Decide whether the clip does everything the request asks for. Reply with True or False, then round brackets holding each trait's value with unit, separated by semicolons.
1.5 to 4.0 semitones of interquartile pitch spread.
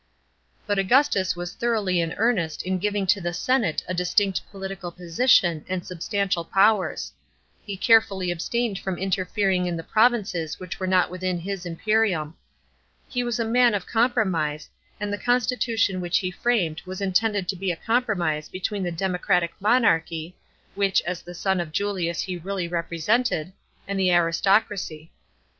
True (3.2 semitones)